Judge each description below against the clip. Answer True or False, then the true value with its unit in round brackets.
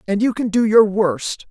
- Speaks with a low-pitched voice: False (210 Hz)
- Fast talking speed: True (240 wpm)